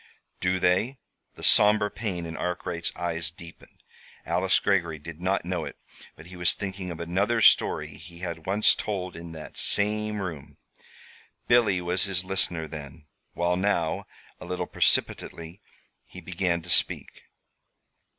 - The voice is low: Yes, very low, 90 Hz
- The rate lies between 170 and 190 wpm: No, average, 145 wpm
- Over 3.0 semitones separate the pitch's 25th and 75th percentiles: No, narrow, 2.6 semitones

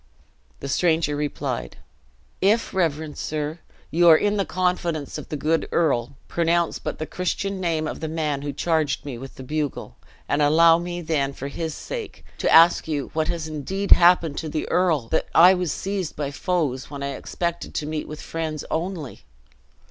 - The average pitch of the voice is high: No, medium, 160 Hz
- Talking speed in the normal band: Yes, average, 180 wpm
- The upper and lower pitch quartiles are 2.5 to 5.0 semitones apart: Yes, average, 2.9 semitones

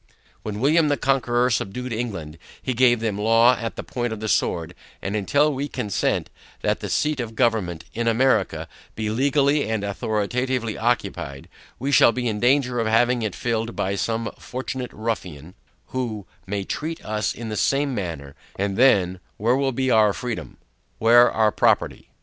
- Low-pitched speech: Yes, low, 115 Hz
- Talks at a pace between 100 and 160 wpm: No, average, 170 wpm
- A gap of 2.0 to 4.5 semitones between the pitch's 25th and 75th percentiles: Yes, average, 3.4 semitones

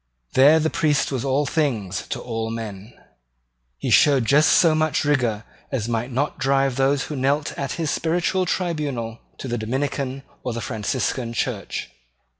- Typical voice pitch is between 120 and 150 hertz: Yes, low, 135 Hz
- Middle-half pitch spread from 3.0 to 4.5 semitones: Yes, average, 4.1 semitones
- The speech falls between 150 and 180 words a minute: Yes, average, 160 wpm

